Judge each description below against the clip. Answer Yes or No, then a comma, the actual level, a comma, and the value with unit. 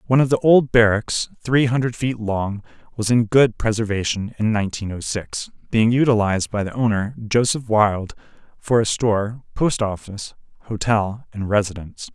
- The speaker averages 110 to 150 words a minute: No, average, 160 wpm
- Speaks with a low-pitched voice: Yes, low, 110 Hz